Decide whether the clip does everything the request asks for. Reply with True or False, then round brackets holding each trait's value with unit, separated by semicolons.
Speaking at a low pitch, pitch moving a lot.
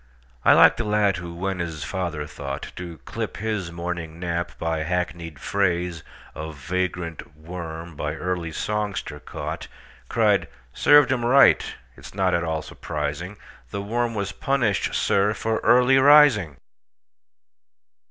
False (90 Hz; 4.4 semitones)